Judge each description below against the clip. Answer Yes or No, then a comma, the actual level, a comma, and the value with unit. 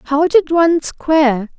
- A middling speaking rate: Yes, average, 150 wpm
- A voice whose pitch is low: No, very high, 310 Hz